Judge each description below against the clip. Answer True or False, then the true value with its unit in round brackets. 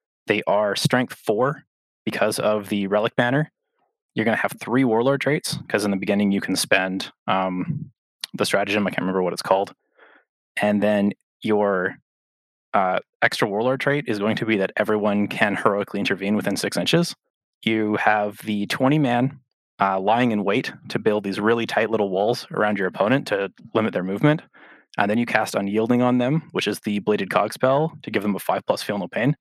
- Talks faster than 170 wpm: True (195 wpm)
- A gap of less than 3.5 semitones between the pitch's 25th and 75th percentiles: False (4.1 semitones)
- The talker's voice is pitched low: True (105 Hz)